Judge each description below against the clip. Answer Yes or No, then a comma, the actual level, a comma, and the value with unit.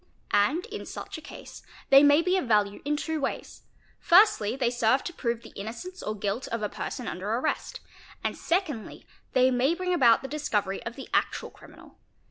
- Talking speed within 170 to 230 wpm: Yes, average, 190 wpm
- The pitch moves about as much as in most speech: No, wide, 6.1 semitones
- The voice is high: Yes, very high, 260 Hz